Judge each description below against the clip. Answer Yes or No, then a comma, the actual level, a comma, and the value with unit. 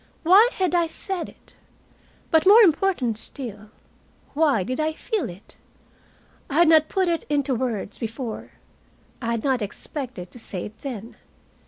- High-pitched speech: Yes, very high, 275 Hz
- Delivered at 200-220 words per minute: No, average, 155 wpm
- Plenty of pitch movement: Yes, wide, 6.7 semitones